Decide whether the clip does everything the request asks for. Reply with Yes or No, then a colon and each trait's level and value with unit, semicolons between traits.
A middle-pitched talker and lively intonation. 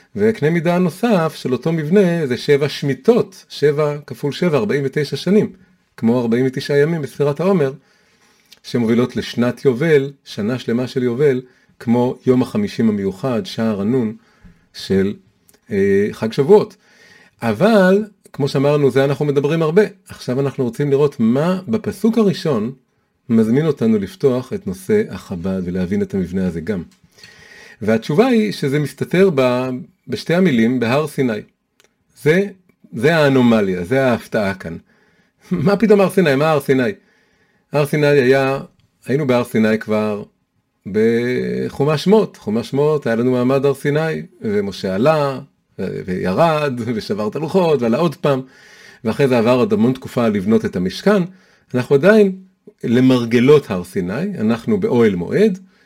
Yes: medium, 150 Hz; wide, 7.9 semitones